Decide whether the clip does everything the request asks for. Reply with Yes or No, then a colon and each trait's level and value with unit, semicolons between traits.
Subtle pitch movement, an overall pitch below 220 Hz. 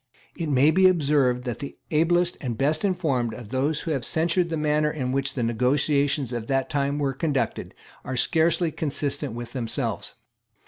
No: average, 3.8 semitones; medium, 140 Hz